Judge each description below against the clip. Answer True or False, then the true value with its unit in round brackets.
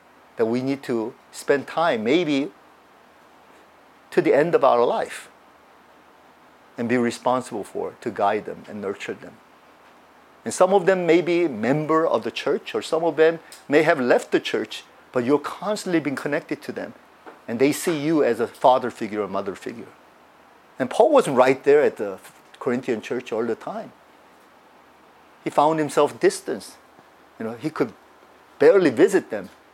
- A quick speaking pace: False (165 wpm)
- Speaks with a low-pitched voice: False (150 Hz)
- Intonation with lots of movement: True (6.0 semitones)